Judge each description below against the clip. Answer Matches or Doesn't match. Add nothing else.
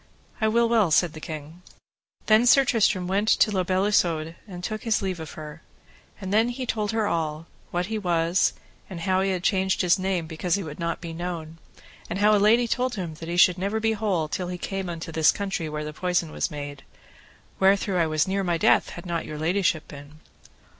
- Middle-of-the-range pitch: Matches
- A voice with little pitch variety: Doesn't match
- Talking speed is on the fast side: Matches